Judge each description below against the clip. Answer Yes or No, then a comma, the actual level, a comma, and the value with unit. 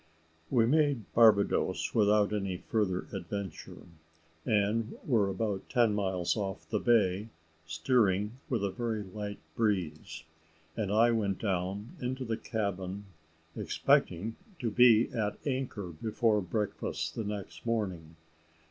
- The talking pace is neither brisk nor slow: No, slow, 120 wpm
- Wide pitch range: No, average, 3.1 semitones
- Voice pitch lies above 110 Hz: No, low, 105 Hz